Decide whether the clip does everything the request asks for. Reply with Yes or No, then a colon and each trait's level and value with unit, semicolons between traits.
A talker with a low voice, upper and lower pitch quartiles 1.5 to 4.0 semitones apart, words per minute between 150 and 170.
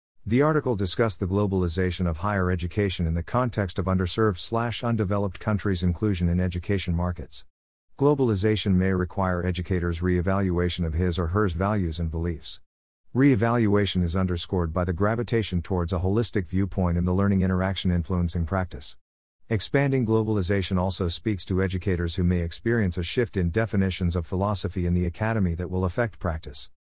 Yes: very low, 95 Hz; average, 2.7 semitones; average, 155 wpm